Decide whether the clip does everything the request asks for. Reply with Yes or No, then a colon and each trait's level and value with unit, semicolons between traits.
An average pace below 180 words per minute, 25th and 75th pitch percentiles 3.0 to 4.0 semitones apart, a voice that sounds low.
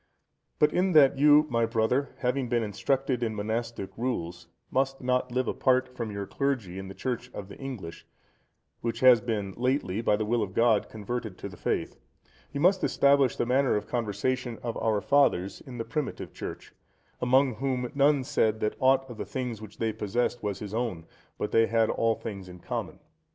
No: average, 190 wpm; average, 3.4 semitones; low, 120 Hz